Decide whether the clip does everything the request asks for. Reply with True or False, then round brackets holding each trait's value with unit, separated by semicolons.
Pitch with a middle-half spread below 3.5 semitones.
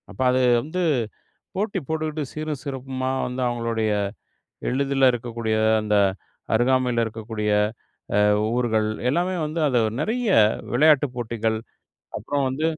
False (4.5 semitones)